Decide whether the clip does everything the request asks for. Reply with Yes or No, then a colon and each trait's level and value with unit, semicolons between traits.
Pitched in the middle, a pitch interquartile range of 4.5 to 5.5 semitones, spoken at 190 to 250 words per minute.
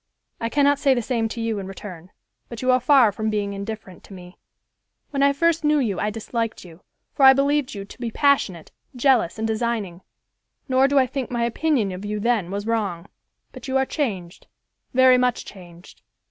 No: high, 230 Hz; average, 5.0 semitones; average, 200 wpm